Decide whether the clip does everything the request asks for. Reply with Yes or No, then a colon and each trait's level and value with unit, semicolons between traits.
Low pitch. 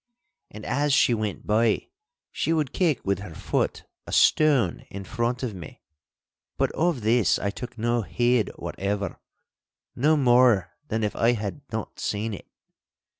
Yes: low, 115 Hz